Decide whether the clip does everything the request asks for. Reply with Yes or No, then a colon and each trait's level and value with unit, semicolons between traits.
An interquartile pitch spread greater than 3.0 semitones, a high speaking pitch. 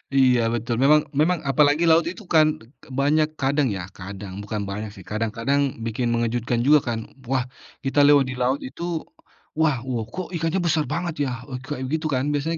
No: average, 4.6 semitones; low, 135 Hz